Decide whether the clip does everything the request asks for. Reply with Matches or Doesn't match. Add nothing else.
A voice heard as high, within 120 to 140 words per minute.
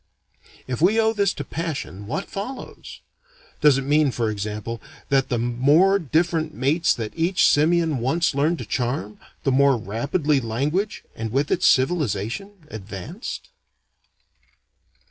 Doesn't match